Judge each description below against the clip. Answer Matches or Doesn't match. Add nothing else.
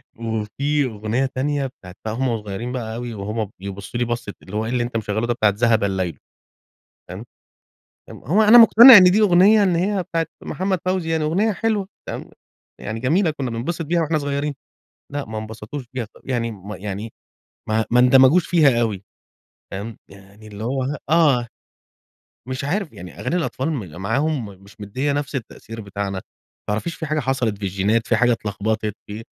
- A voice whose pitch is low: Matches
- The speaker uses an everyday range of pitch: Doesn't match